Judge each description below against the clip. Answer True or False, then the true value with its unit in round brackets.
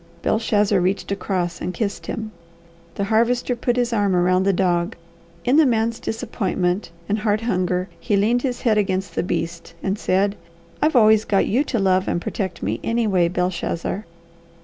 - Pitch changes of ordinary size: True (3.7 semitones)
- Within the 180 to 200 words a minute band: False (170 wpm)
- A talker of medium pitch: False (200 Hz)